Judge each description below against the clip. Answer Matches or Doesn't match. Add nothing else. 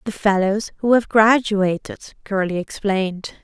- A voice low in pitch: Doesn't match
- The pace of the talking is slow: Matches